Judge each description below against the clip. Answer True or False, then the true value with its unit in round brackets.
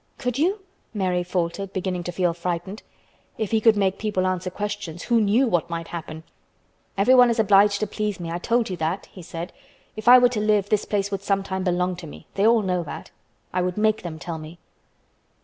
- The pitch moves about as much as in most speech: True (3.3 semitones)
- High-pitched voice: True (195 Hz)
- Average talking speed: False (210 wpm)